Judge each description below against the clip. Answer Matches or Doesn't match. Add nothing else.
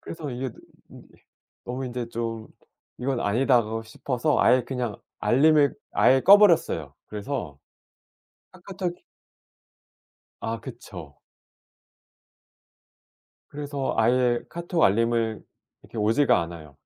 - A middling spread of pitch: Matches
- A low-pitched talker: Matches